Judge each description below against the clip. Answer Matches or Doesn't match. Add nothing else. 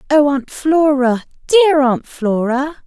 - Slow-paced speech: Matches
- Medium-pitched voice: Doesn't match